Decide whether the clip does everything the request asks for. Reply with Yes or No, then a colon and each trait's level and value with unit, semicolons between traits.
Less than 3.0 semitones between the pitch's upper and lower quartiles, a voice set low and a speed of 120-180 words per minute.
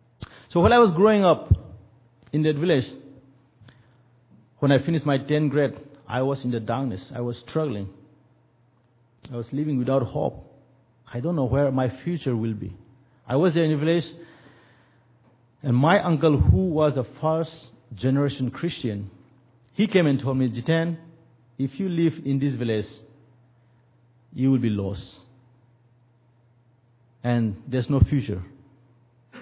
No: average, 3.3 semitones; low, 130 Hz; average, 145 wpm